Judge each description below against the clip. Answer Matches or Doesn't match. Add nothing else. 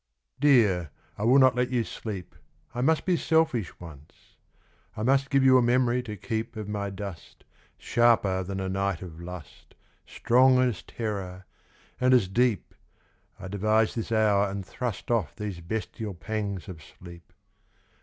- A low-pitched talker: Matches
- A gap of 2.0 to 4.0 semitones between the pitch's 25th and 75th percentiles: Doesn't match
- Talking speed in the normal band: Matches